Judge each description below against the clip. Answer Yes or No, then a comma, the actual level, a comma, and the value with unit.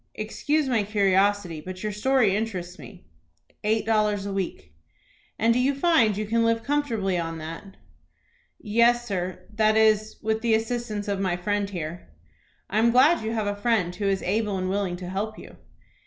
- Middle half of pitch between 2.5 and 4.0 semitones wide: Yes, average, 2.9 semitones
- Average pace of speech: Yes, average, 180 wpm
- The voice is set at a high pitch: Yes, high, 210 Hz